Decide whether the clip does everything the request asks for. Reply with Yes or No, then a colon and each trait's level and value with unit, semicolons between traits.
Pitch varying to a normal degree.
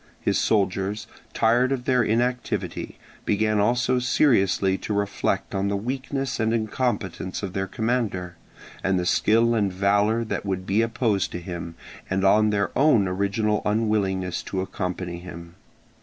Yes: average, 3.3 semitones